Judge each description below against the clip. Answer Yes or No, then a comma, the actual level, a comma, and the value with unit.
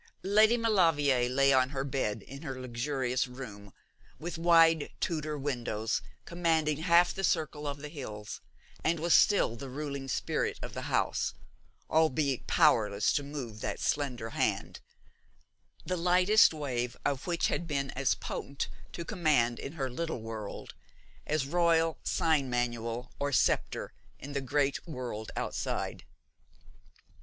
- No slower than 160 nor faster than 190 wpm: No, average, 140 wpm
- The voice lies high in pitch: No, medium, 140 Hz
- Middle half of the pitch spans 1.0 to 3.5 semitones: No, average, 4.6 semitones